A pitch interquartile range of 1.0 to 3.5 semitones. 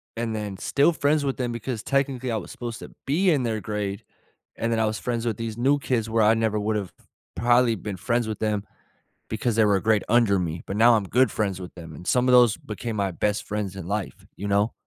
Yes: average, 2.9 semitones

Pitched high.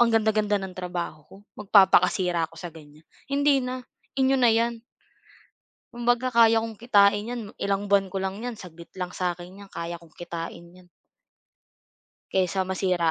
Yes: high, 195 Hz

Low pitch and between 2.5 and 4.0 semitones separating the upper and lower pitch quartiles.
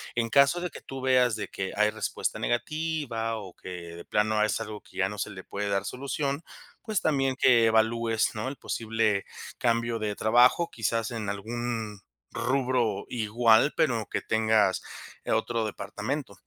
Yes: low, 115 Hz; average, 3.0 semitones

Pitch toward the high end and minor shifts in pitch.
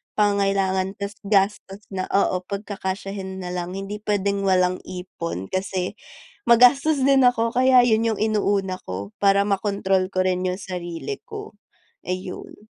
Yes: high, 195 Hz; narrow, 2.3 semitones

